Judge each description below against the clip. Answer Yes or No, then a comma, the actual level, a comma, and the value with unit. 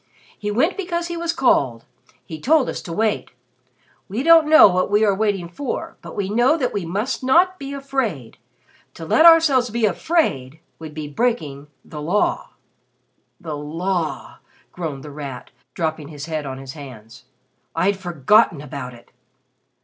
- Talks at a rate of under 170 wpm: Yes, average, 160 wpm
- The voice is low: No, high, 190 Hz